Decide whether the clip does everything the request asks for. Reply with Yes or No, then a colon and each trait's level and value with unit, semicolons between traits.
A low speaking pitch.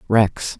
Yes: low, 105 Hz